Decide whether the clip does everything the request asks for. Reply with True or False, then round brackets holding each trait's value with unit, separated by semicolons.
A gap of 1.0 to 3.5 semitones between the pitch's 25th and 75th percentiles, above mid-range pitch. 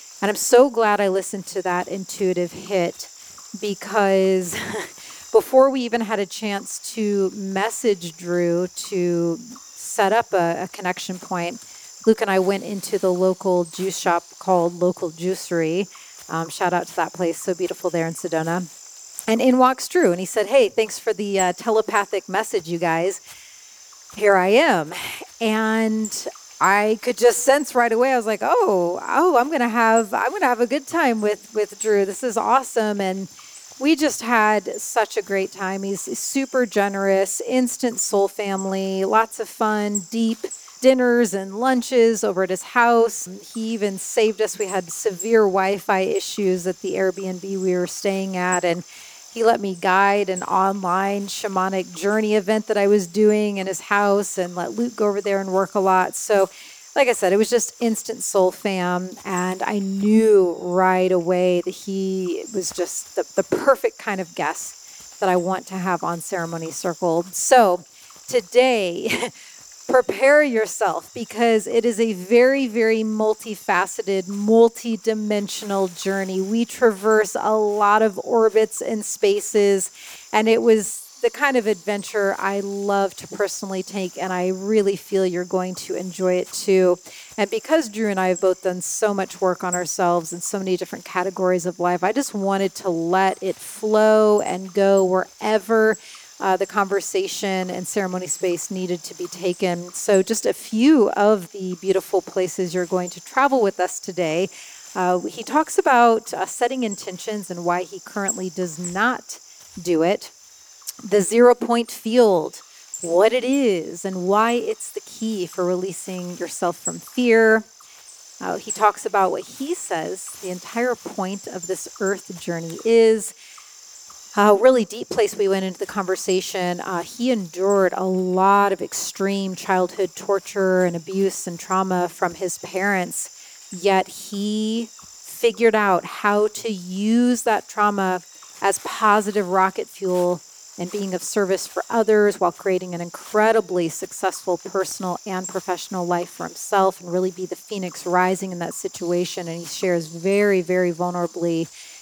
True (3.2 semitones; 195 Hz)